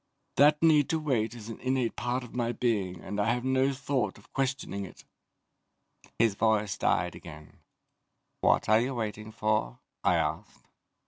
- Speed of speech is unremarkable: Yes, average, 160 wpm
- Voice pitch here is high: No, low, 115 Hz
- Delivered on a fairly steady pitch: No, average, 4.0 semitones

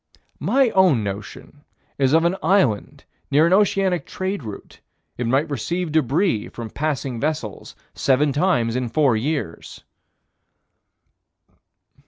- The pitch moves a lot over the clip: Yes, wide, 6.7 semitones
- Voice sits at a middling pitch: Yes, medium, 145 Hz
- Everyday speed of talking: No, slow, 120 wpm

